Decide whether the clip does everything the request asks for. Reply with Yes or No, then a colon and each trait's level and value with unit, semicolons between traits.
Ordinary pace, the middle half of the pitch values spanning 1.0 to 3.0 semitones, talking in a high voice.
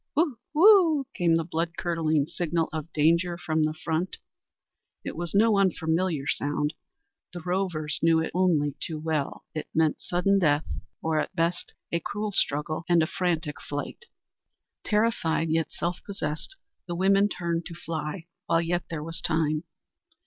No: average, 150 wpm; narrow, 2.6 semitones; medium, 165 Hz